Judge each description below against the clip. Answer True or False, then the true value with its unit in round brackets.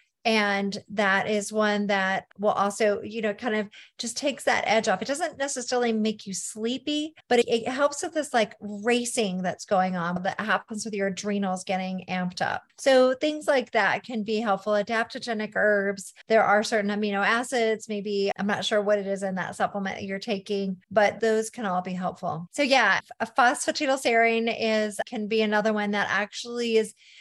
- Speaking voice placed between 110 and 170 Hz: False (215 Hz)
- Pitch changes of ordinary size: True (3.1 semitones)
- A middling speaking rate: True (190 wpm)